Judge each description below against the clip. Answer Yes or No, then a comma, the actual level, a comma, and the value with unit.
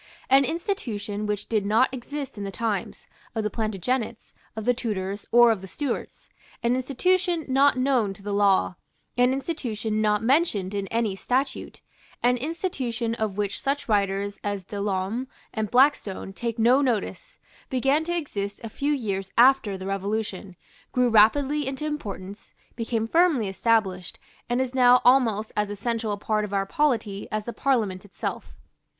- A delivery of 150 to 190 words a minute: Yes, average, 160 wpm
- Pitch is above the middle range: Yes, high, 225 Hz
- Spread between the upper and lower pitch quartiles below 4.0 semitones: No, average, 4.5 semitones